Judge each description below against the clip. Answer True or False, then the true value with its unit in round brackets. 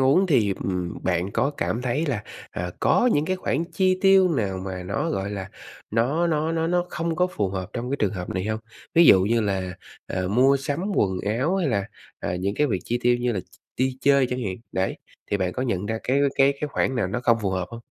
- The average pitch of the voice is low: True (120 Hz)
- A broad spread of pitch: True (7.1 semitones)